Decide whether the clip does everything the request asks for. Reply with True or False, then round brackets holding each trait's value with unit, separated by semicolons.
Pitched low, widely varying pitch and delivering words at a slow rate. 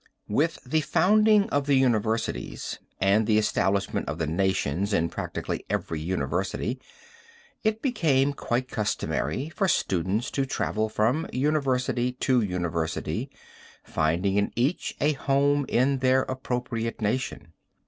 True (125 Hz; 6.1 semitones; 125 wpm)